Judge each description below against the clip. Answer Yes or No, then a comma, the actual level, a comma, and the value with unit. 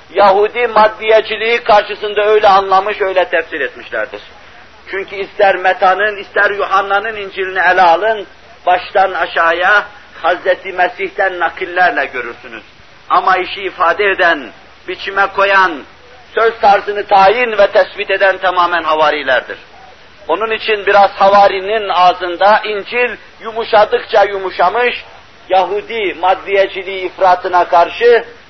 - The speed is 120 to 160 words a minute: No, average, 100 wpm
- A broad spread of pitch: No, narrow, 2.5 semitones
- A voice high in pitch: Yes, high, 195 Hz